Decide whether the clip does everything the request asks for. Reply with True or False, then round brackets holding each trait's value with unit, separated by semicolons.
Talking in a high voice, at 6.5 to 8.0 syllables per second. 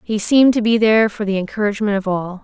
True (210 Hz; 6.9 syllables/s)